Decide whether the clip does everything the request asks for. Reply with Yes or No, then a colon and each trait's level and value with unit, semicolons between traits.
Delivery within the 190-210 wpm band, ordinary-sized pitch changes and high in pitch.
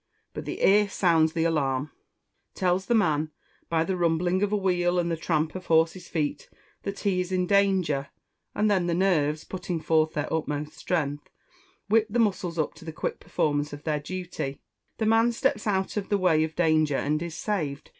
No: average, 195 wpm; average, 3.6 semitones; medium, 170 Hz